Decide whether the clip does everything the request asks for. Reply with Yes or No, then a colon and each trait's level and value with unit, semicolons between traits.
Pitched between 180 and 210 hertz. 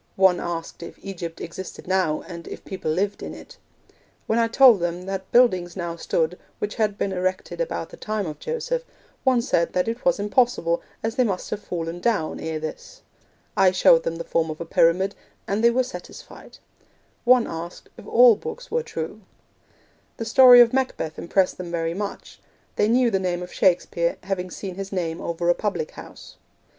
Yes: high, 190 Hz